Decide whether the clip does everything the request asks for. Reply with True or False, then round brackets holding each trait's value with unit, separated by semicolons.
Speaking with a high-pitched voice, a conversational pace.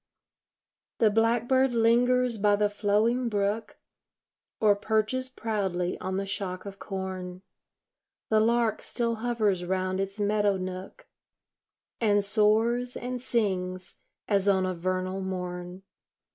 False (205 Hz; 115 wpm)